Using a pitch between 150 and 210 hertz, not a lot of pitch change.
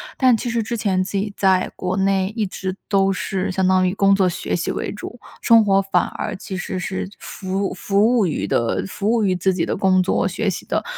Yes: high, 195 Hz; narrow, 1.8 semitones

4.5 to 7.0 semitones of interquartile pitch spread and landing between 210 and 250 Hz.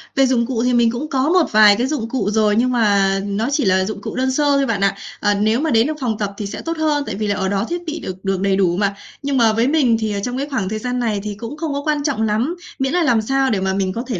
Yes: average, 4.9 semitones; high, 230 Hz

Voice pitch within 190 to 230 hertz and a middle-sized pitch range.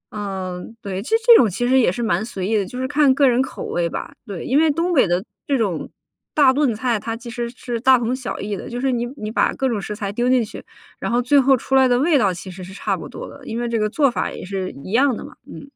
No: high, 240 Hz; average, 4.4 semitones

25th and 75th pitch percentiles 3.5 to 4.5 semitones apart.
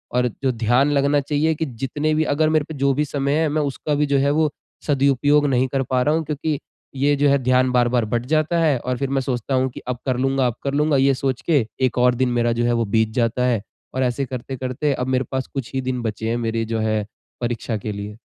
No: average, 2.8 semitones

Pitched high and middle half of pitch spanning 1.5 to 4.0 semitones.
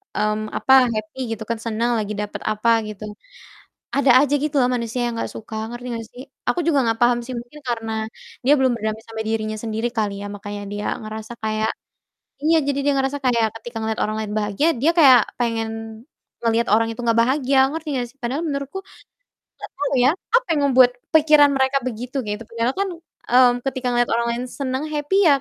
Yes: high, 240 Hz; average, 3.5 semitones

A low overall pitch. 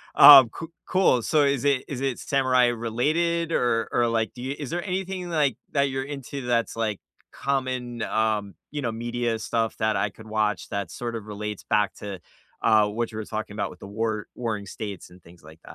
Yes: low, 115 Hz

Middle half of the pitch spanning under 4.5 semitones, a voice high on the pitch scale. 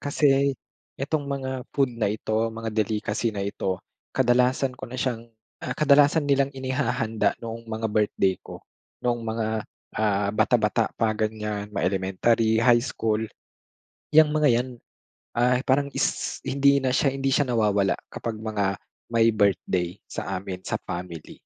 No: average, 3.8 semitones; low, 115 Hz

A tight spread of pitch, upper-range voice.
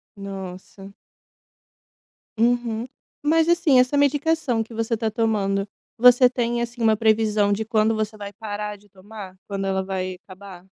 No: average, 3.2 semitones; high, 220 Hz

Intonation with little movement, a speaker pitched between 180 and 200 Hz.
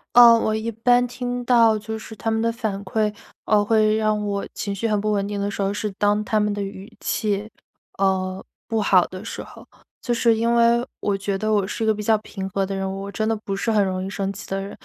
No: narrow, 2.1 semitones; high, 210 Hz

